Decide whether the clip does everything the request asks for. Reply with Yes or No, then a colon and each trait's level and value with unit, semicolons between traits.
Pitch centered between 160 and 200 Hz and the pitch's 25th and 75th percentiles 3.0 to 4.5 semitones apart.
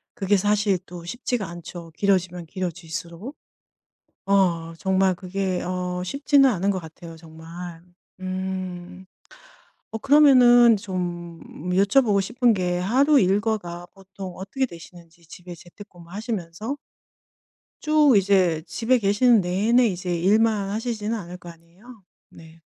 Yes: high, 190 Hz; average, 3.8 semitones